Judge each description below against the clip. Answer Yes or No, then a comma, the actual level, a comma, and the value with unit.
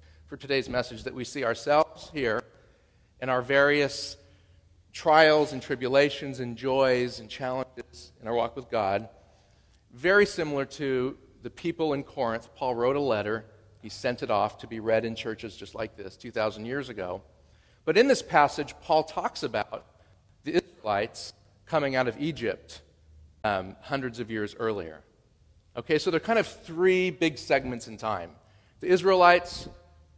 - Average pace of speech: Yes, average, 155 wpm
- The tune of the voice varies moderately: No, wide, 5.9 semitones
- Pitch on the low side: Yes, low, 120 Hz